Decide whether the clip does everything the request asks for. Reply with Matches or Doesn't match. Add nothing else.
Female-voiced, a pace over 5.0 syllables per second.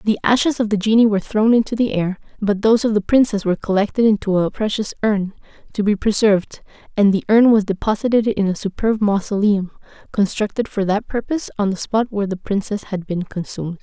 Matches